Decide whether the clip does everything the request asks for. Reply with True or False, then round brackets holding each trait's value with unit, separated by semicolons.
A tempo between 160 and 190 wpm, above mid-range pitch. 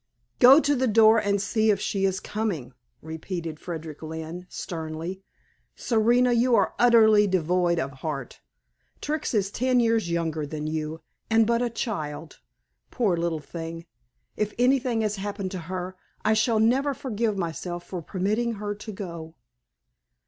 False (150 wpm; 195 Hz)